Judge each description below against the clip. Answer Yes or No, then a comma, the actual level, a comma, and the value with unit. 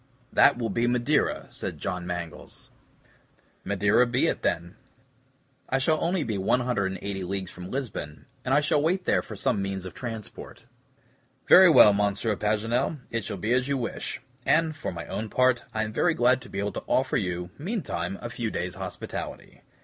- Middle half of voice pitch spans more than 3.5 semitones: Yes, average, 5.2 semitones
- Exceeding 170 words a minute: Yes, average, 180 wpm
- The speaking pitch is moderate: No, low, 115 Hz